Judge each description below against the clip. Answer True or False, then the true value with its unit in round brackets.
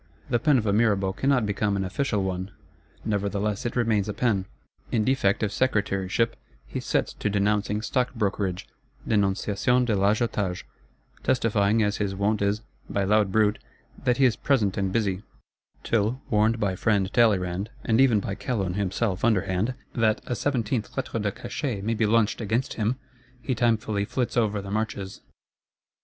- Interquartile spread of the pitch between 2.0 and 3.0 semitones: True (2.6 semitones)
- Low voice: True (105 Hz)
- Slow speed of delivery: False (160 wpm)